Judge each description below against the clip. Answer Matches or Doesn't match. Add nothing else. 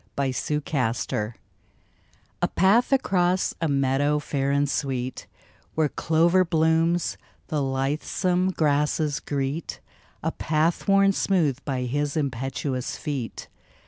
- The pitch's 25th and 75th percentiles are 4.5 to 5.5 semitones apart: Doesn't match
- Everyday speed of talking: Doesn't match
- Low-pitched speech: Doesn't match